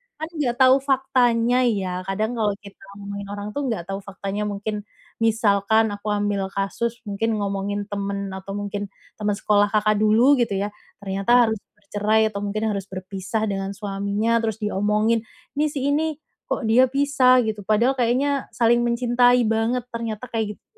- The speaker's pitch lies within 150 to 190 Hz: No, high, 215 Hz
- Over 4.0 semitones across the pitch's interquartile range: No, average, 3.0 semitones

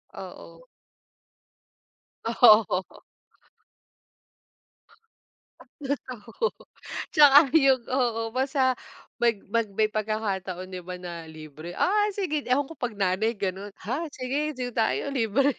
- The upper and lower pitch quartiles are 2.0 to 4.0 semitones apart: No, wide, 5.5 semitones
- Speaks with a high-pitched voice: Yes, high, 235 Hz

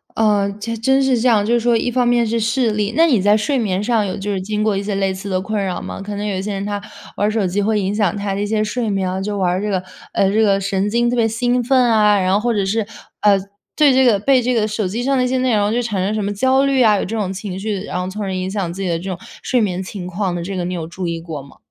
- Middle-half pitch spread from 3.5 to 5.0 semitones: No, average, 3.1 semitones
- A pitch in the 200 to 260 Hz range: Yes, high, 210 Hz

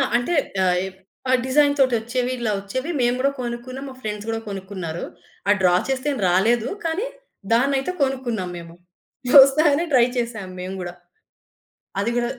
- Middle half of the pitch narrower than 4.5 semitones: No, average, 4.9 semitones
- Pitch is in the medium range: No, high, 240 Hz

